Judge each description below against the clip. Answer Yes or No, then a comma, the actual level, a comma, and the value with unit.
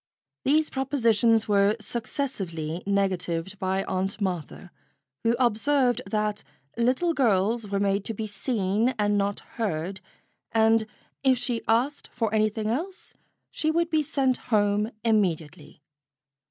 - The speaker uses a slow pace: Yes, slow, 125 wpm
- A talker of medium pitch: No, high, 215 Hz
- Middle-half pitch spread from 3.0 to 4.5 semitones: Yes, average, 3.8 semitones